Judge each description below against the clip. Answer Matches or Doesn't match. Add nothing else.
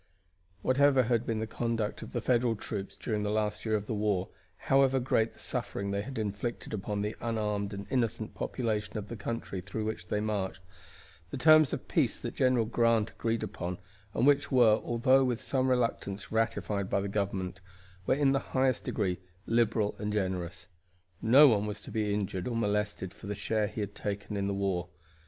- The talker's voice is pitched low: Matches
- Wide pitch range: Doesn't match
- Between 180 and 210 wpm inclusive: Matches